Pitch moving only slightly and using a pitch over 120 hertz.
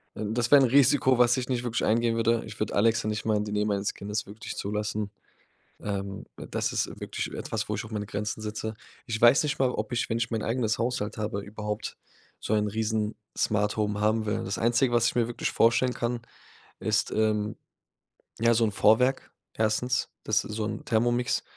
No: narrow, 2.0 semitones; low, 110 Hz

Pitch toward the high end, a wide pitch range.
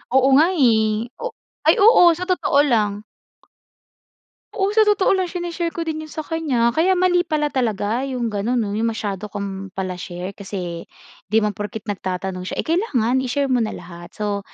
Yes: high, 235 Hz; wide, 7.7 semitones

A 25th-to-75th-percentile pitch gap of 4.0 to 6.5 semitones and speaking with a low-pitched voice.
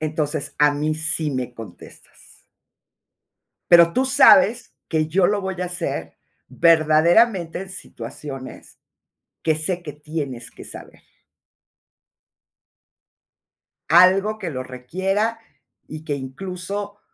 No: average, 4.5 semitones; medium, 165 Hz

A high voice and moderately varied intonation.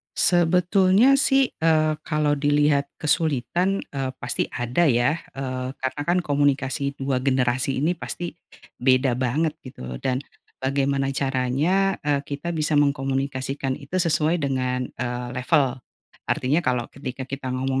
No: medium, 140 Hz; average, 3.3 semitones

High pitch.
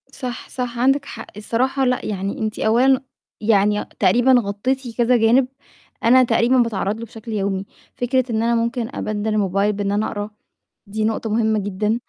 Yes: high, 225 Hz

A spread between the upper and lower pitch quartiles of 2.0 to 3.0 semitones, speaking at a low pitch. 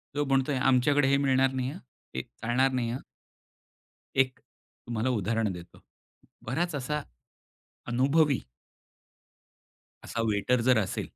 Yes: narrow, 2.6 semitones; low, 130 Hz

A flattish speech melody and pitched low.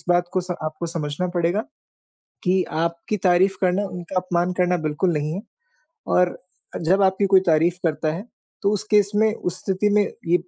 No: narrow, 2.2 semitones; medium, 180 Hz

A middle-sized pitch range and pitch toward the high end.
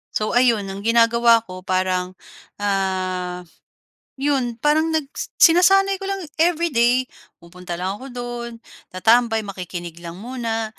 No: wide, 5.7 semitones; high, 230 Hz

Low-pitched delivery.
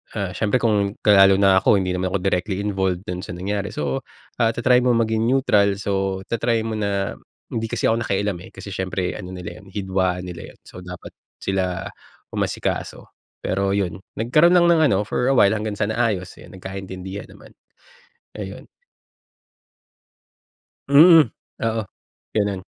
Yes: low, 100 Hz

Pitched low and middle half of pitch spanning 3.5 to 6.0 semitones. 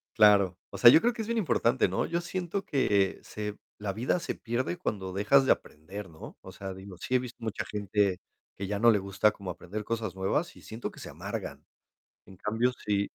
Yes: low, 105 Hz; average, 4.2 semitones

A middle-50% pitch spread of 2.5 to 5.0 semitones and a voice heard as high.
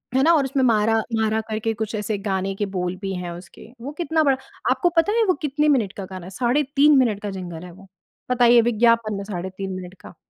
No: wide, 5.5 semitones; high, 220 Hz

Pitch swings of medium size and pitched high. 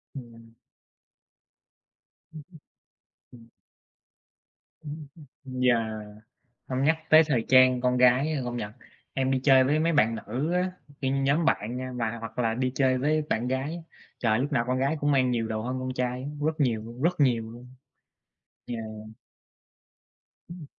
No: average, 3.3 semitones; low, 130 Hz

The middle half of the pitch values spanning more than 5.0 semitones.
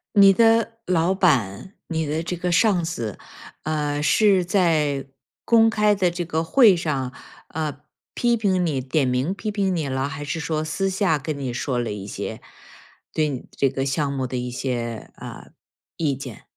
Yes: wide, 5.6 semitones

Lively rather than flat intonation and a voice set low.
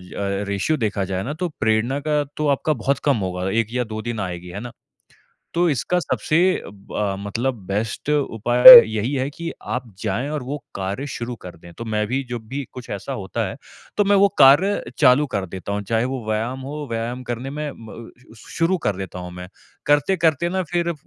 Yes: wide, 6.1 semitones; low, 120 Hz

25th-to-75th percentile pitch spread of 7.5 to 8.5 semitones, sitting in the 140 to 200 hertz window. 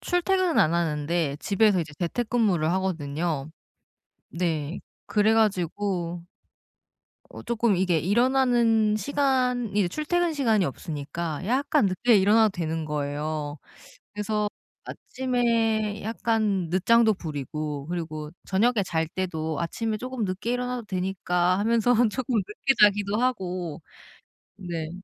No: wide, 5.6 semitones; high, 195 Hz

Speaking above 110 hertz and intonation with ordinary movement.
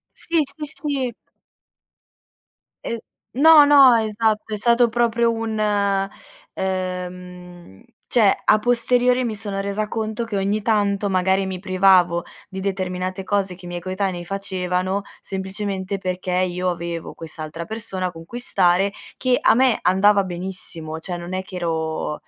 Yes: high, 190 Hz; average, 3.3 semitones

